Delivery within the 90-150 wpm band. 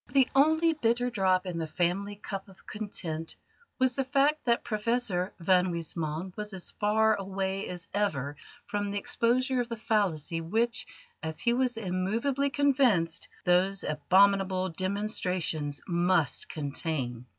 Yes: average, 140 wpm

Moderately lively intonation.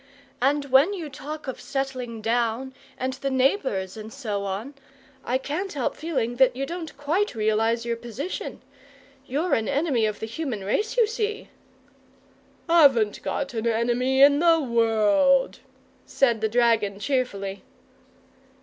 Yes: average, 4.2 semitones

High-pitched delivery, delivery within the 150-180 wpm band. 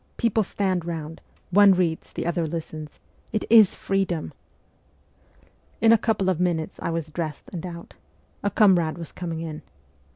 No: medium, 175 Hz; average, 160 wpm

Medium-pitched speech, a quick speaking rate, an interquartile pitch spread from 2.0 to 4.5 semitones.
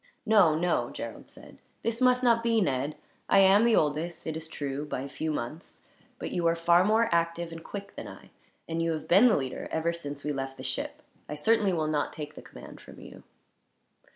No: medium, 165 Hz; fast, 215 wpm; average, 5.0 semitones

